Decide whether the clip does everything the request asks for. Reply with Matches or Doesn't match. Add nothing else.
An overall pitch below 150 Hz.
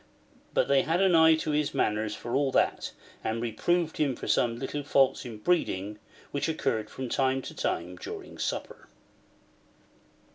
Matches